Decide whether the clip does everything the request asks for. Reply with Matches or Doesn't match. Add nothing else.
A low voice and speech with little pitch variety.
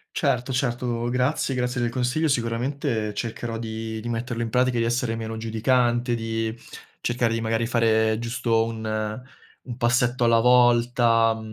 Matches